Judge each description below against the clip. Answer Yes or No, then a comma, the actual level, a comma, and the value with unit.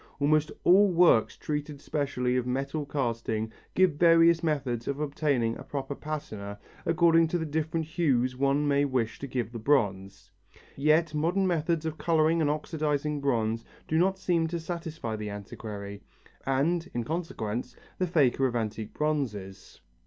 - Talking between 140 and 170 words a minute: Yes, average, 155 wpm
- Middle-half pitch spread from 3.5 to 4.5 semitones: No, average, 5.3 semitones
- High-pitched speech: No, medium, 145 Hz